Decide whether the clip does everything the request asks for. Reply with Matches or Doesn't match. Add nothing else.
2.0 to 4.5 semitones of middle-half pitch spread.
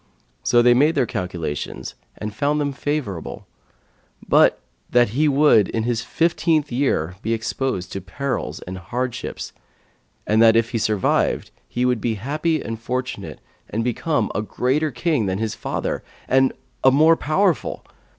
Doesn't match